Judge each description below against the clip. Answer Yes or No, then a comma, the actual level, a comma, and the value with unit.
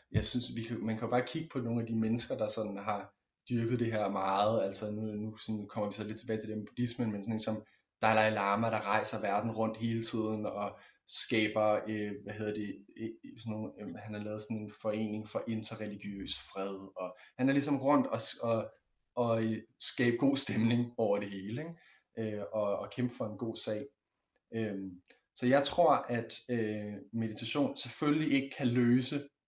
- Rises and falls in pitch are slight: Yes, narrow, 2.2 semitones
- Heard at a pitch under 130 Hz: Yes, low, 110 Hz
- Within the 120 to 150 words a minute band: No, average, 195 wpm